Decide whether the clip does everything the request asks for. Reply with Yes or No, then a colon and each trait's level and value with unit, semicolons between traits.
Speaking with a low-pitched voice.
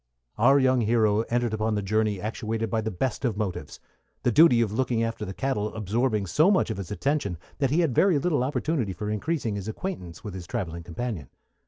Yes: low, 110 Hz